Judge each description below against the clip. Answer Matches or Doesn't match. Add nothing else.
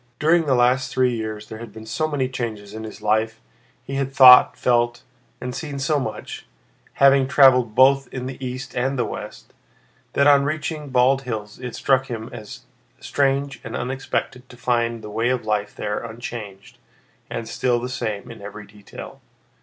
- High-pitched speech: Doesn't match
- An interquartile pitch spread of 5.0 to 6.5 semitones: Doesn't match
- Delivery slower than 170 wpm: Doesn't match